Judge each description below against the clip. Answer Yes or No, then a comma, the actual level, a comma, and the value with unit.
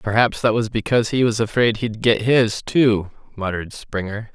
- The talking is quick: No, average, 180 wpm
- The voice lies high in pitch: No, low, 110 Hz